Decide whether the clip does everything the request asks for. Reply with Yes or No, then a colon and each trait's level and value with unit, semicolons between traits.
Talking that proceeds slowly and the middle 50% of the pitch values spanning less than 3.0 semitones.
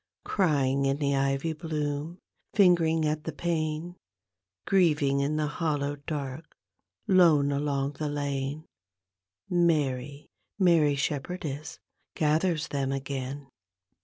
Yes: slow, 105 wpm; narrow, 2.6 semitones